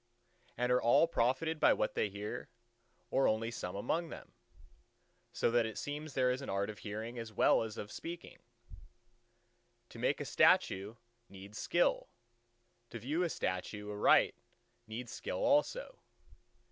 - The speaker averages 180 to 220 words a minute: No, average, 150 wpm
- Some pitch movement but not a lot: No, wide, 5.7 semitones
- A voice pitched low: Yes, low, 115 Hz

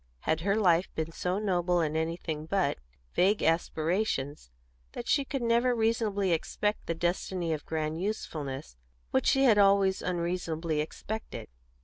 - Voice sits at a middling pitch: Yes, medium, 175 Hz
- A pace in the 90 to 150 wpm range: Yes, average, 140 wpm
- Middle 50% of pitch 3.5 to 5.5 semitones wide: Yes, average, 4.3 semitones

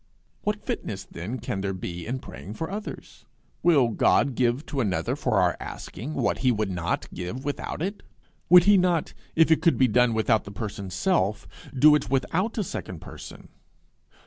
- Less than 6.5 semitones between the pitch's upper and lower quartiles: No, wide, 8.2 semitones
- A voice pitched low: Yes, low, 125 Hz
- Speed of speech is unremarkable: Yes, average, 180 wpm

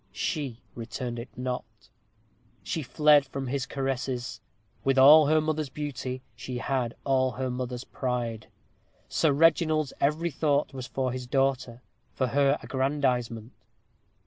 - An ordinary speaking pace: No, slow, 130 wpm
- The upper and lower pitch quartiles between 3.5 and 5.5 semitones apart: No, narrow, 2.5 semitones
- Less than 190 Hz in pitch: Yes, low, 135 Hz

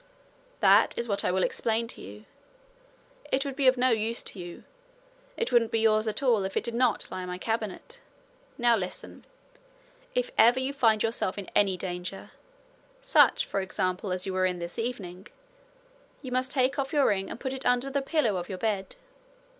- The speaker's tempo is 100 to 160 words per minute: No, average, 200 wpm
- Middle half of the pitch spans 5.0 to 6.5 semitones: Yes, wide, 5.4 semitones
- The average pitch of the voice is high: Yes, high, 225 Hz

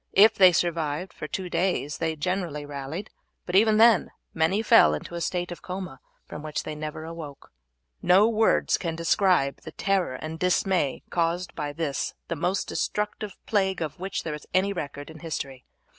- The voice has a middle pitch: Yes, medium, 170 Hz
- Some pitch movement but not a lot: Yes, average, 4.0 semitones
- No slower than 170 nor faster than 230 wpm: Yes, average, 175 wpm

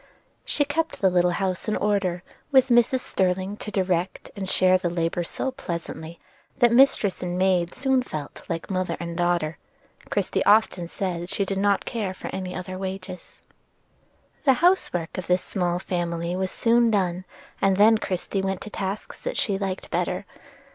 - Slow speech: No, average, 175 wpm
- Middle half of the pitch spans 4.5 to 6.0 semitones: No, average, 2.9 semitones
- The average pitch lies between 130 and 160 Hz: No, medium, 185 Hz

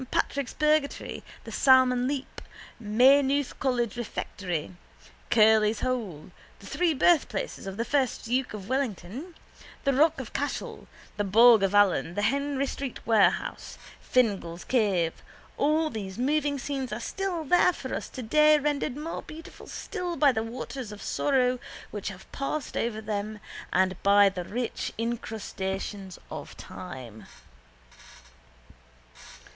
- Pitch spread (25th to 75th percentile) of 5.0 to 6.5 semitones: Yes, wide, 5.4 semitones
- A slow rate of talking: Yes, slow, 130 wpm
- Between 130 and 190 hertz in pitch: No, high, 245 Hz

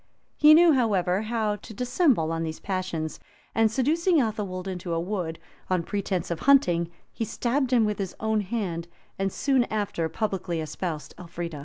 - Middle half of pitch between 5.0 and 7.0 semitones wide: Yes, wide, 5.4 semitones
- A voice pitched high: Yes, high, 200 Hz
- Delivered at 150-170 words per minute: Yes, average, 160 wpm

